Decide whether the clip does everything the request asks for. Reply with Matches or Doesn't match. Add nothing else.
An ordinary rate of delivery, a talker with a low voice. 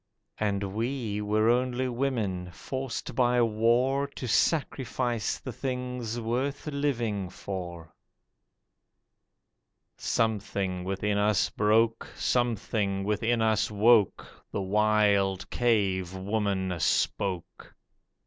Doesn't match